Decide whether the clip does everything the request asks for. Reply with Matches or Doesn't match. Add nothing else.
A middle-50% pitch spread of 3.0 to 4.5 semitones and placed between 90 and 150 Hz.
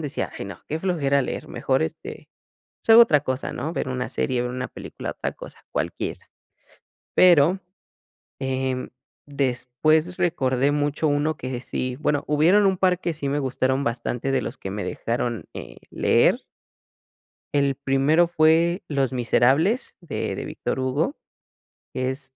Matches